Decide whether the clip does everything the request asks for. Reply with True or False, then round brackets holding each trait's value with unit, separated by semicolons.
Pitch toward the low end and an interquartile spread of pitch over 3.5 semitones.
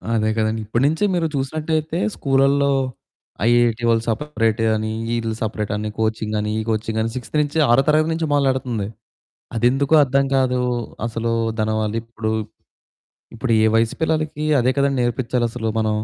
True (120 Hz; 3.9 semitones)